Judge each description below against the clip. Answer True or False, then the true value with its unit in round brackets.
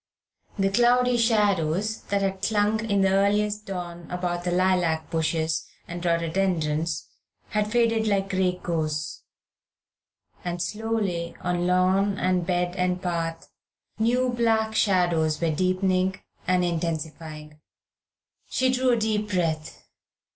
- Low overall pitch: False (185 Hz)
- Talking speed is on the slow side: True (120 wpm)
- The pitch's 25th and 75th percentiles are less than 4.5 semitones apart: True (3.7 semitones)